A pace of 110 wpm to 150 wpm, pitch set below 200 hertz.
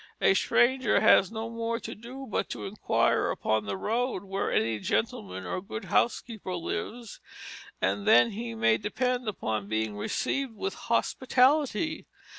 No: average, 145 wpm; high, 220 Hz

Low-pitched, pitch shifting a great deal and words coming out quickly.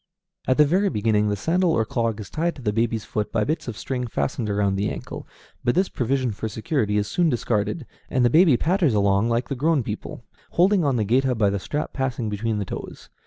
Yes: low, 120 Hz; wide, 5.8 semitones; fast, 225 wpm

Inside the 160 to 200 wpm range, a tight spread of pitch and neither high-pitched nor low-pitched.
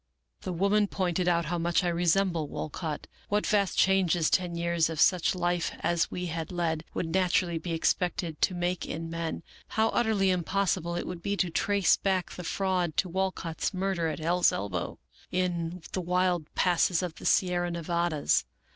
Yes: average, 175 wpm; narrow, 2.0 semitones; medium, 175 Hz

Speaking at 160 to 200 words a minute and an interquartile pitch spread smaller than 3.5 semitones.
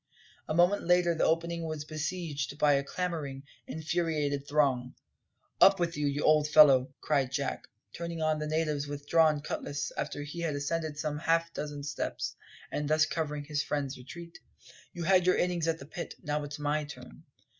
Yes: average, 175 wpm; narrow, 2.5 semitones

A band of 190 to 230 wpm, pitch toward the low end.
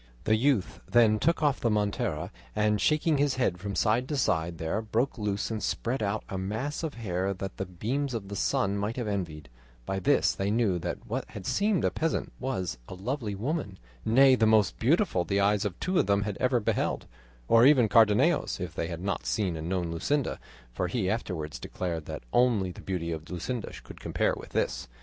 Yes: fast, 205 wpm; low, 105 Hz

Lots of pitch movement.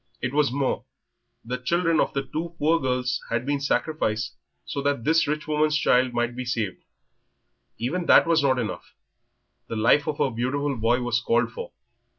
No: average, 3.9 semitones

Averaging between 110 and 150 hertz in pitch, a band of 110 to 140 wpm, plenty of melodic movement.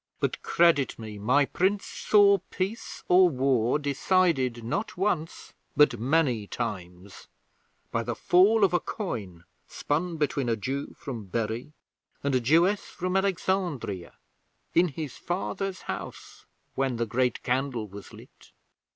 Yes: medium, 140 Hz; slow, 135 wpm; wide, 7.5 semitones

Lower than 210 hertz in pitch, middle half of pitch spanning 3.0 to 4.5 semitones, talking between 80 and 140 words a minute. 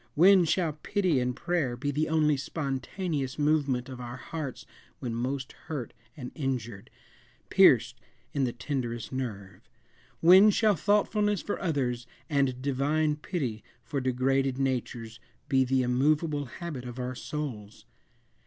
Yes: low, 135 Hz; average, 3.8 semitones; slow, 135 wpm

